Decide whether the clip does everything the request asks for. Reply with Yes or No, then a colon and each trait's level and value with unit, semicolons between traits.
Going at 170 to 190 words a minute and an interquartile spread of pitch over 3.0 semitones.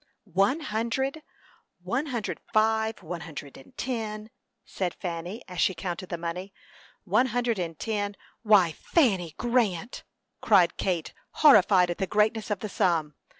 No: average, 150 wpm; average, 4.4 semitones